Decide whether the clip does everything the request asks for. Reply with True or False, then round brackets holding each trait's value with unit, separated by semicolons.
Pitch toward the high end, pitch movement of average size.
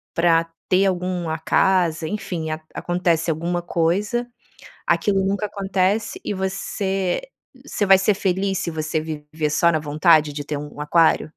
False (175 Hz; 3.3 semitones)